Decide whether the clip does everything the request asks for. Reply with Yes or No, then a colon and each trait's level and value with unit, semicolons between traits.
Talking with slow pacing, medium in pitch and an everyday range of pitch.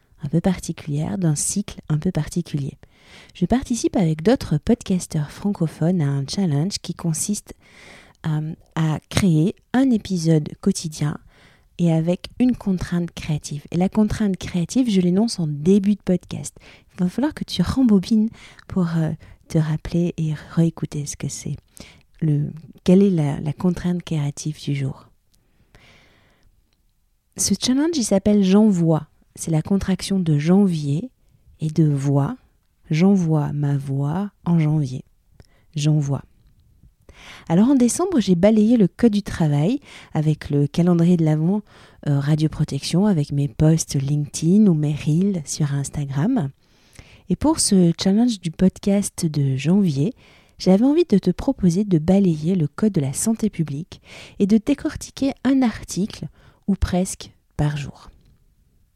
Yes: slow, 140 wpm; medium, 170 Hz; average, 4.8 semitones